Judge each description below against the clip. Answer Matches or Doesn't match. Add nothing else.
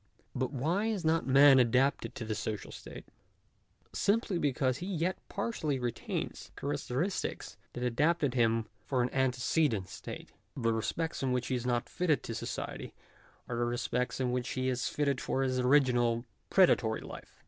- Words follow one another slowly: Doesn't match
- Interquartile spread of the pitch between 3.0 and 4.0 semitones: Matches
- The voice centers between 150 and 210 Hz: Doesn't match